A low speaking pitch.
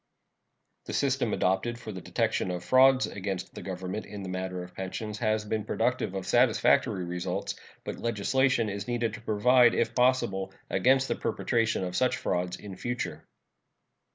Yes: low, 105 Hz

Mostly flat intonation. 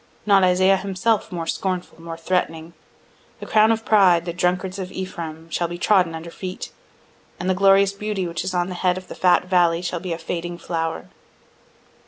Yes: narrow, 2.0 semitones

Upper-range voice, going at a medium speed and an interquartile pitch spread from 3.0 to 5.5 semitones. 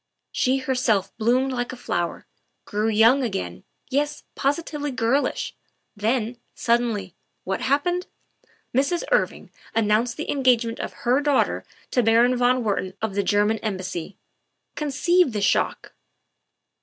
No: high, 240 Hz; slow, 130 wpm; average, 4.1 semitones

